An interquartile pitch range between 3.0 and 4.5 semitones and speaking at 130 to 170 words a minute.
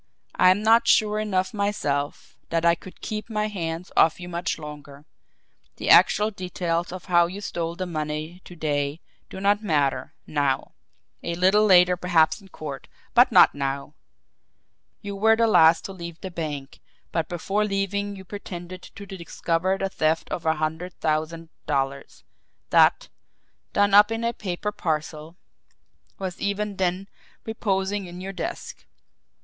Yes: average, 3.9 semitones; average, 155 wpm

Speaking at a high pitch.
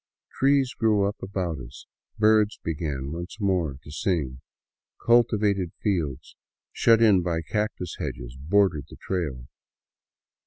No: very low, 90 Hz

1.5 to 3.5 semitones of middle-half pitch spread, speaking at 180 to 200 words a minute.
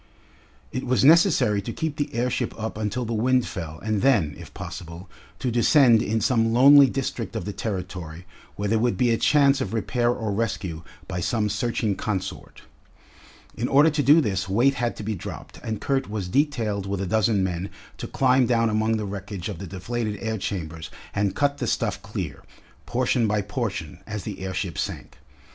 No: average, 4.2 semitones; average, 190 wpm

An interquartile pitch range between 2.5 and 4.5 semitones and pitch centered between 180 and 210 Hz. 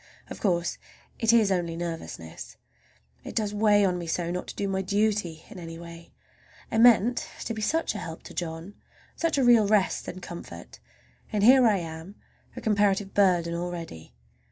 Yes: average, 3.9 semitones; high, 190 Hz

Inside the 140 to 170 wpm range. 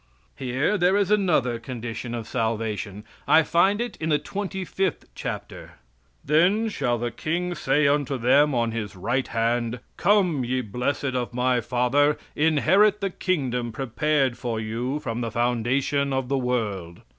Yes: average, 150 wpm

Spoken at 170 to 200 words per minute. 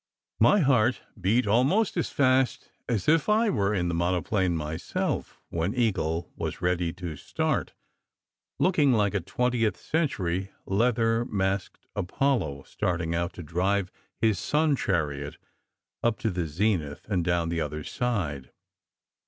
No: average, 140 wpm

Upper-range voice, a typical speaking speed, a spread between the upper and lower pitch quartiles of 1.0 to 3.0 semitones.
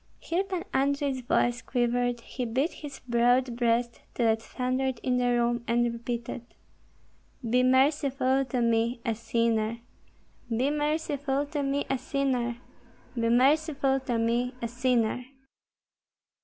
No: very high, 250 Hz; slow, 130 wpm; narrow, 2.5 semitones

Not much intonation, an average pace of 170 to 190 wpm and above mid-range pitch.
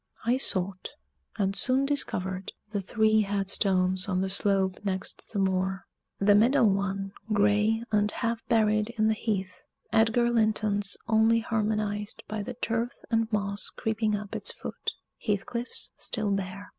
No: narrow, 2.2 semitones; average, 145 wpm; high, 210 Hz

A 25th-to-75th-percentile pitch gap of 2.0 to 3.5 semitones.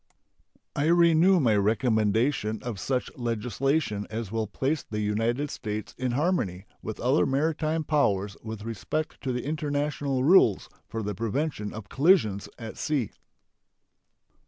No: wide, 5.6 semitones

